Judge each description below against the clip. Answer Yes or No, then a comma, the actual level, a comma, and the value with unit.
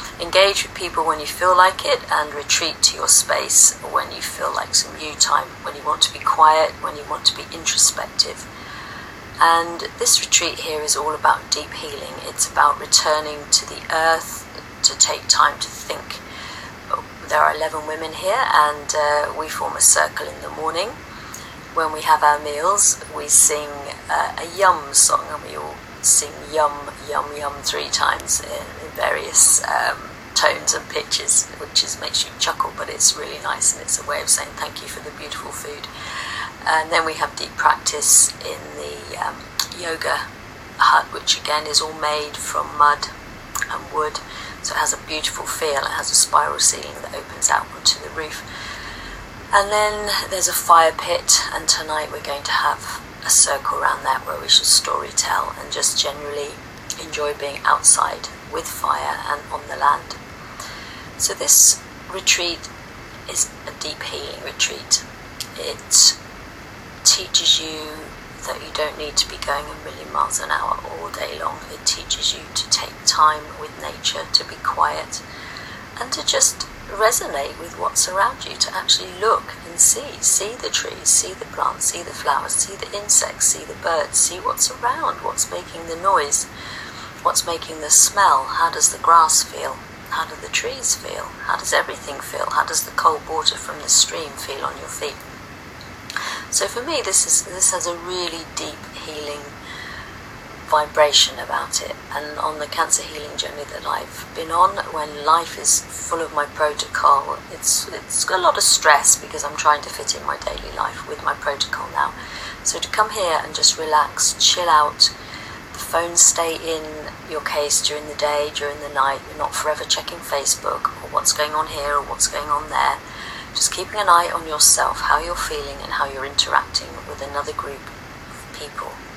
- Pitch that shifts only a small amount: Yes, narrow, 2.0 semitones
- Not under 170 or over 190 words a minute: Yes, average, 180 wpm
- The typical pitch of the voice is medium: Yes, medium, 150 Hz